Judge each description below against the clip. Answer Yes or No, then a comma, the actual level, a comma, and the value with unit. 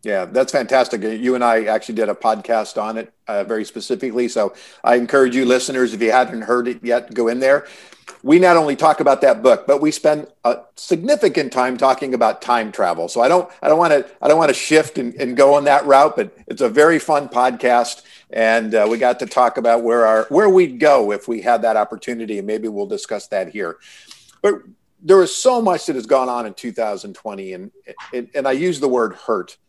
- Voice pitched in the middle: No, low, 125 Hz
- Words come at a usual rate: No, fast, 230 wpm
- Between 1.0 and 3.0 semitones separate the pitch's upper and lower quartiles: No, average, 3.7 semitones